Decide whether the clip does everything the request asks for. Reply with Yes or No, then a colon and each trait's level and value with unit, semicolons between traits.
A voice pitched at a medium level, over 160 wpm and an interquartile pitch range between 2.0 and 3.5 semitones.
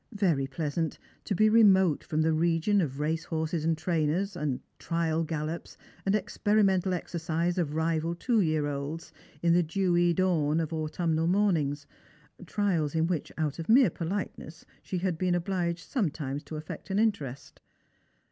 No: medium, 165 Hz; average, 150 wpm; average, 3.1 semitones